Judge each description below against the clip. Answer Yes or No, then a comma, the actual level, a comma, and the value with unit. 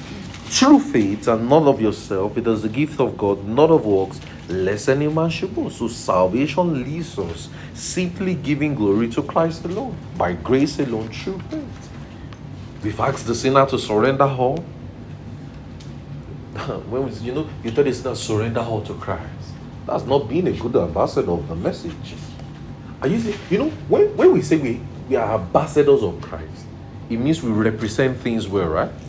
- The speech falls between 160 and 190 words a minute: Yes, average, 175 wpm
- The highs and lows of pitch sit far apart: Yes, wide, 5.7 semitones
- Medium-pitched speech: No, low, 130 Hz